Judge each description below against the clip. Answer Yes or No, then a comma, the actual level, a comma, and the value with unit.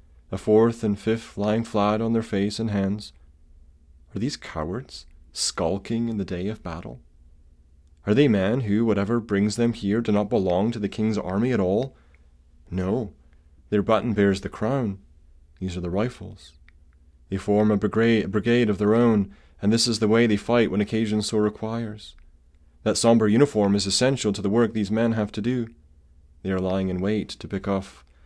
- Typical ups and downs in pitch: No, wide, 6.3 semitones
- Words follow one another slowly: No, average, 185 wpm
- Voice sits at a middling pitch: No, low, 100 Hz